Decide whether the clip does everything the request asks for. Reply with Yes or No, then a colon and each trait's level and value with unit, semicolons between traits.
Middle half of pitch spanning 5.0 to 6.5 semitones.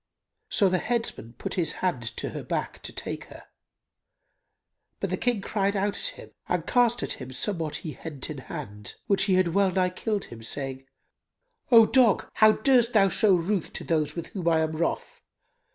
Yes: average, 5.3 semitones